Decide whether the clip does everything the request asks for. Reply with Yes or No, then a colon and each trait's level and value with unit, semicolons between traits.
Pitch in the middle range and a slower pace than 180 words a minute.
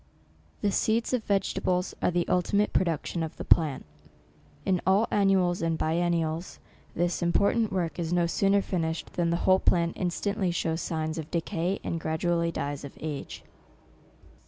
Yes: medium, 175 Hz; average, 155 wpm